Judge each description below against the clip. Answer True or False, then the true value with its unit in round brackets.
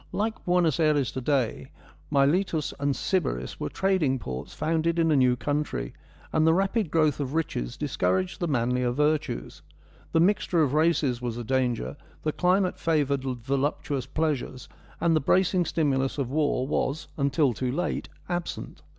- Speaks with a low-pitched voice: False (145 Hz)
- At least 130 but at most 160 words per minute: True (155 wpm)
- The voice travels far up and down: False (4.1 semitones)